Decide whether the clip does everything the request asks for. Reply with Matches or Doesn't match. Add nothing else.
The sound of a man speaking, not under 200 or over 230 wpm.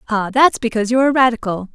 Doesn't match